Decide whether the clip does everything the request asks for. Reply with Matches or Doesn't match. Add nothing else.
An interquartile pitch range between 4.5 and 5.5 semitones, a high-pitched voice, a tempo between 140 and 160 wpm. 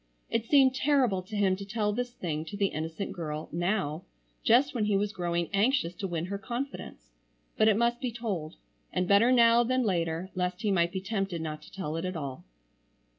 Doesn't match